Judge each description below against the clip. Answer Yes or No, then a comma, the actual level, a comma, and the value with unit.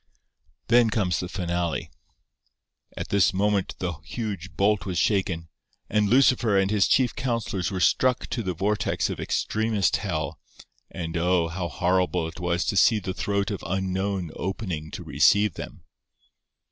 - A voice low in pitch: Yes, very low, 95 Hz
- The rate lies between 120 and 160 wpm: Yes, average, 150 wpm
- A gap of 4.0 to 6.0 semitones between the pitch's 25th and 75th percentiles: No, average, 3.1 semitones